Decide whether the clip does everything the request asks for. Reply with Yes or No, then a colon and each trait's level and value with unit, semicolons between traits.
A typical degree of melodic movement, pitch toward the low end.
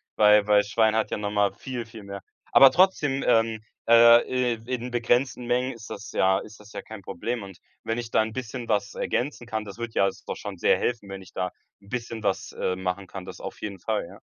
Yes: average, 3.0 semitones; low, 110 Hz